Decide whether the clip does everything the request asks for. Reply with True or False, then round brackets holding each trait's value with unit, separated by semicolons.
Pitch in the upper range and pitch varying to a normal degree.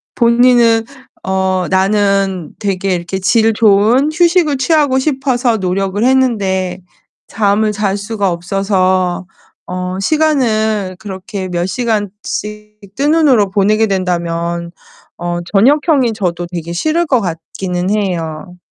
True (200 Hz; 4.3 semitones)